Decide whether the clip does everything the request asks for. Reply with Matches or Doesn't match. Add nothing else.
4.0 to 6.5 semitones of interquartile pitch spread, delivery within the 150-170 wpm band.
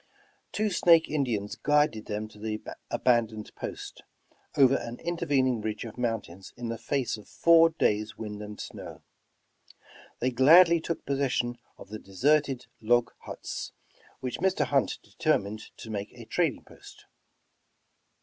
Doesn't match